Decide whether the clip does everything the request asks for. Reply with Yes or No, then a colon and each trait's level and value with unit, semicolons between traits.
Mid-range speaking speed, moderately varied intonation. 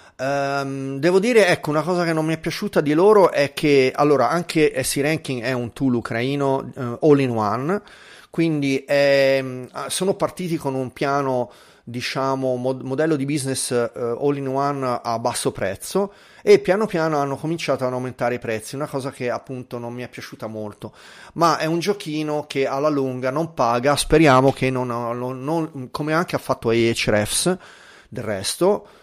No: fast, 175 wpm; average, 3.6 semitones